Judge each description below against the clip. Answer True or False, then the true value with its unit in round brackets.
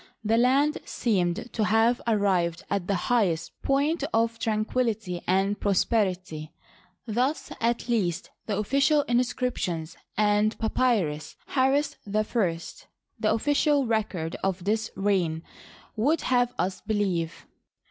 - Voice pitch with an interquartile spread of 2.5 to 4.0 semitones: False (4.8 semitones)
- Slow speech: True (115 wpm)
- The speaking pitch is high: True (215 Hz)